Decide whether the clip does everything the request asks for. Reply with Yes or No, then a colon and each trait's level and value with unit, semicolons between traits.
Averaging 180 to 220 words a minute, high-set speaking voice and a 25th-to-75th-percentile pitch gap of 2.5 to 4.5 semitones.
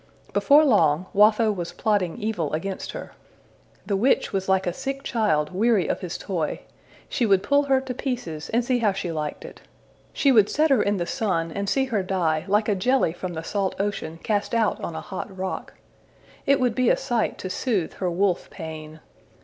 No: average, 200 wpm; high, 200 Hz; average, 5.1 semitones